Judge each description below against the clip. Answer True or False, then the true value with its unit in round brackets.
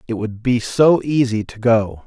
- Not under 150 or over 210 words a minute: True (205 wpm)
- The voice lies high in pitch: False (115 Hz)